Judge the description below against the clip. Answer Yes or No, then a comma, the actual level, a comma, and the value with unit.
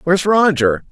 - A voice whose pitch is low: No, medium, 170 Hz